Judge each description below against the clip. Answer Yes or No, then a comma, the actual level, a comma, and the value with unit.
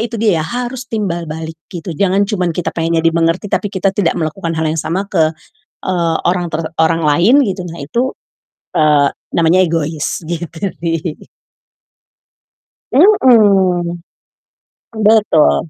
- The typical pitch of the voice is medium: Yes, medium, 170 Hz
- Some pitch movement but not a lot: Yes, average, 3.7 semitones